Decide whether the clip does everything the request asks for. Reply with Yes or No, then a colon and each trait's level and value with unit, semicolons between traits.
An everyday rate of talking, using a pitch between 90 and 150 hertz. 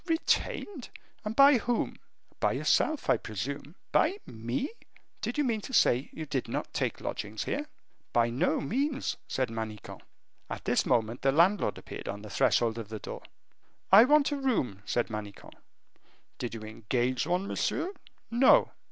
Yes: average, 160 wpm; medium, 140 Hz